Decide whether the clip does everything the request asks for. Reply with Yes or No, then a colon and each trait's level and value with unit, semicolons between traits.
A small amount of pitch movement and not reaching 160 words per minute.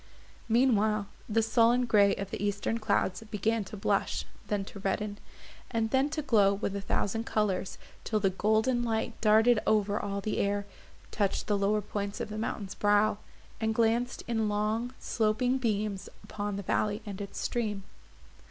No: narrow, 1.9 semitones; average, 165 wpm